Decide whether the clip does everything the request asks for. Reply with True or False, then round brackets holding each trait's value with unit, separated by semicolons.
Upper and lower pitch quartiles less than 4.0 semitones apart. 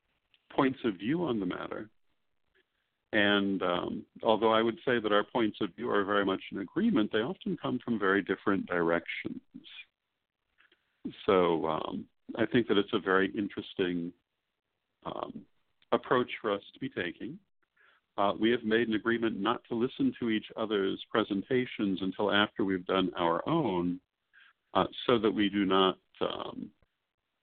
True (3.1 semitones)